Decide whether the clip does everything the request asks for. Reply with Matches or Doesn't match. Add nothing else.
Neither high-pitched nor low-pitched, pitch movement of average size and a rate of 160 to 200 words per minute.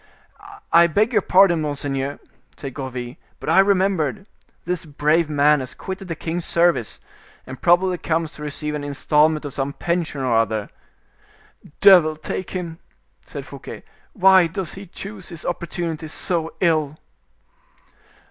Doesn't match